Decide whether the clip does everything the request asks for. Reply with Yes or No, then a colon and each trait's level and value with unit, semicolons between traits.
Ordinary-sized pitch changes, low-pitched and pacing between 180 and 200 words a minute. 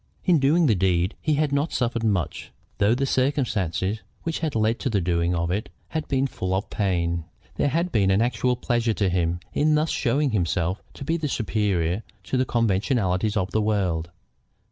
No: wide, 6.5 semitones; low, 110 Hz; average, 190 wpm